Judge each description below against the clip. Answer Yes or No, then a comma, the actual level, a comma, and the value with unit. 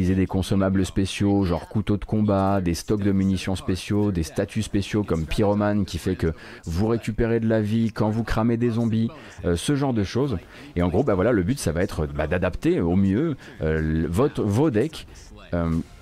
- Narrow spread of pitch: No, average, 3.8 semitones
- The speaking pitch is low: Yes, low, 100 Hz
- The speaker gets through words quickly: No, average, 205 wpm